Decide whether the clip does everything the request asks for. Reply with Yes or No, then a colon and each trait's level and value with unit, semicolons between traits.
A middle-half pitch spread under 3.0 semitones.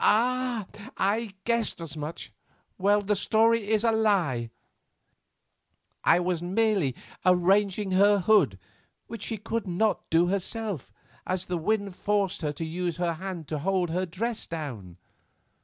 No: average, 4.1 semitones